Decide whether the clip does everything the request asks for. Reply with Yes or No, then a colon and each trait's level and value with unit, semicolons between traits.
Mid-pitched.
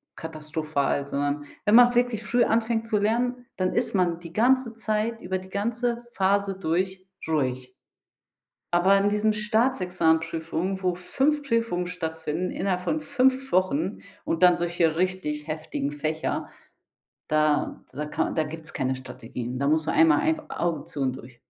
Yes: medium, 180 Hz